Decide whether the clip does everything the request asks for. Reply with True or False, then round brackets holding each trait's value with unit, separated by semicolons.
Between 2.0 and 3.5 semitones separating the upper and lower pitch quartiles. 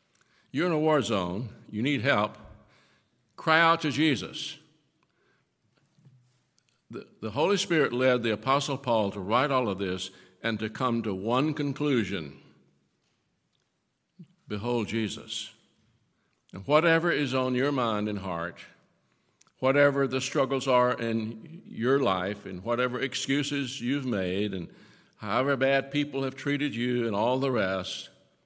False (5.1 semitones)